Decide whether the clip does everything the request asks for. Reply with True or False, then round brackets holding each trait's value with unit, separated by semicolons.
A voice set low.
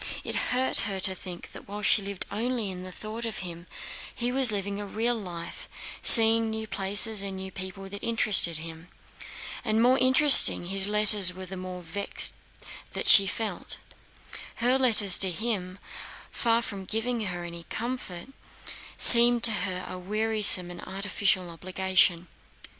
False (200 Hz)